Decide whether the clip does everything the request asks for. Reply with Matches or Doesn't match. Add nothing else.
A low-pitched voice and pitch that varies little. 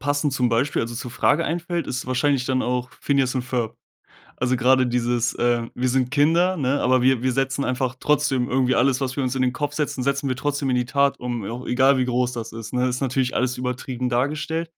Matches